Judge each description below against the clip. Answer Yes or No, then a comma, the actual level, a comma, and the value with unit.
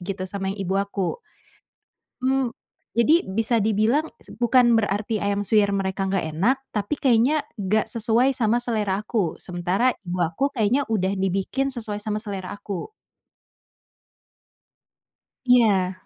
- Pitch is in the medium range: No, high, 210 Hz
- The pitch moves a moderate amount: Yes, average, 3.8 semitones